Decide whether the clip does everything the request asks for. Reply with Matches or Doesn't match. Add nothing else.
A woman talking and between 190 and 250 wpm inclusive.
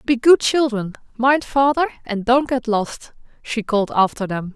Doesn't match